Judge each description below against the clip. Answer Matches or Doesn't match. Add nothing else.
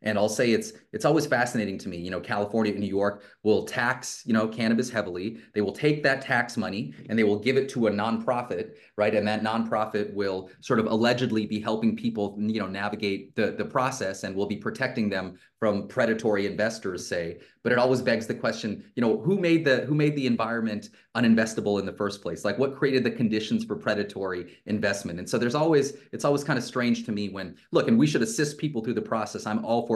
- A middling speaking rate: Doesn't match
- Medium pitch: Doesn't match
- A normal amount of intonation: Matches